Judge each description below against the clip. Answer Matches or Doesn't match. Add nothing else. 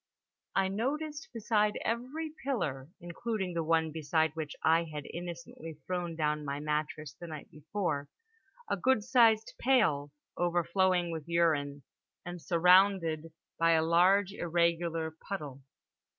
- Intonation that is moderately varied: Matches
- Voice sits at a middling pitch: Matches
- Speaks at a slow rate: Matches